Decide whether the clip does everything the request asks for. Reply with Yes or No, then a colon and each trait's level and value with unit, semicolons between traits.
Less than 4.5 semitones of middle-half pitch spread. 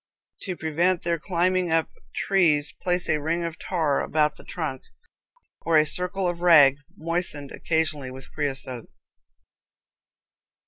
Yes: average, 3.1 semitones